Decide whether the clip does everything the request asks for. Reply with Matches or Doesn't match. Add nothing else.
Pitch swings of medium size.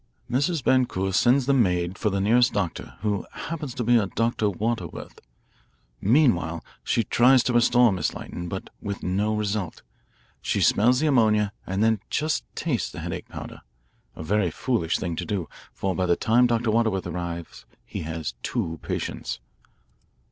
Matches